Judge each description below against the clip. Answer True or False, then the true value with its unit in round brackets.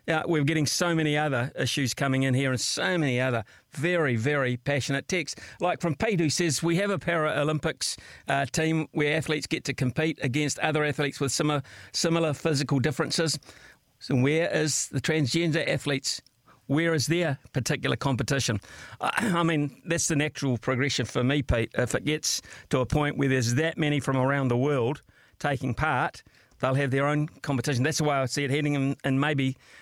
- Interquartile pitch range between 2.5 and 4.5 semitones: True (3.0 semitones)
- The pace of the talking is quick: False (185 wpm)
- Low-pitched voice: False (145 Hz)